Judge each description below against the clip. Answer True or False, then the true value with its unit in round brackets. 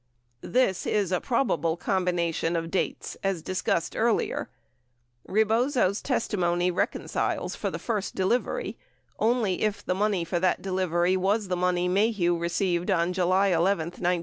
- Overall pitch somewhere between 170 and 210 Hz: True (185 Hz)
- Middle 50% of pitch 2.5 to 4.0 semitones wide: True (2.9 semitones)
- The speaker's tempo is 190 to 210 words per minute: False (145 wpm)